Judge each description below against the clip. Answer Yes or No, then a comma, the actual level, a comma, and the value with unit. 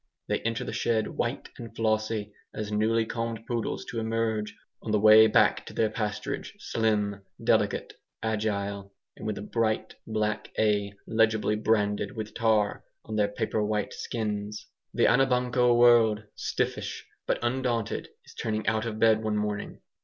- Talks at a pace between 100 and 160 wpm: Yes, average, 150 wpm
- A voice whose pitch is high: No, low, 110 Hz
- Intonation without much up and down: Yes, narrow, 1.3 semitones